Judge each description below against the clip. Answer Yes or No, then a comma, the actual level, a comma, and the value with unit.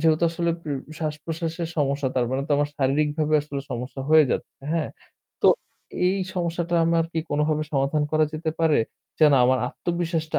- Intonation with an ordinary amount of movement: No, narrow, 2.2 semitones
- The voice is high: No, medium, 155 Hz